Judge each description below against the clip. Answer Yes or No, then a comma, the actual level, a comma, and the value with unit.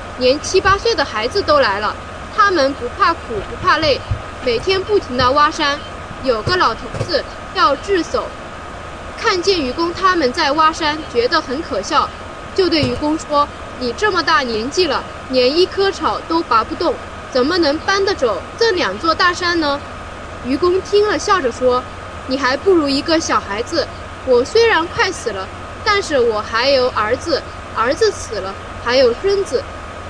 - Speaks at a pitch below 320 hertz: No, very high, 335 Hz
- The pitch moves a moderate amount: No, wide, 6.1 semitones